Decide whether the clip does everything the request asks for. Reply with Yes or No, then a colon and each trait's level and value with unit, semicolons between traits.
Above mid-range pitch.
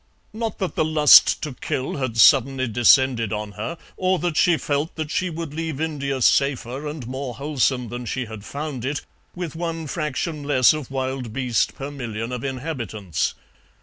No: low, 135 Hz